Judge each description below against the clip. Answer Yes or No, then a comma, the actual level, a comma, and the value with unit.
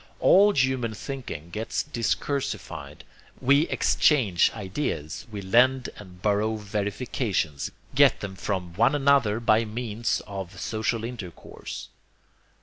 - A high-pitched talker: No, low, 110 Hz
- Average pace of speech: No, slow, 110 wpm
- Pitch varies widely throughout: No, average, 4.7 semitones